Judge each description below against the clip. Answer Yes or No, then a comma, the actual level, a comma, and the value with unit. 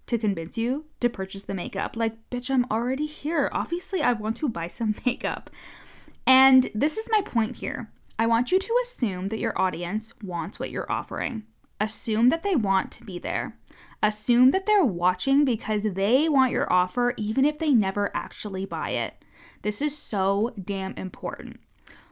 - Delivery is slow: No, average, 175 wpm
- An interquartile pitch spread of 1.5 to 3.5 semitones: No, average, 4.8 semitones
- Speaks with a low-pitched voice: No, high, 230 Hz